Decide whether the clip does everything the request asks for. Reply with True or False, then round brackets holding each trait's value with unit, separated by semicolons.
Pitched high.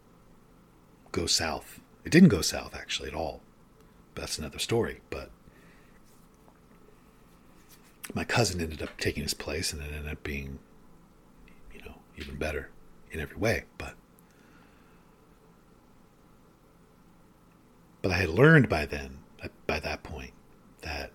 False (80 Hz)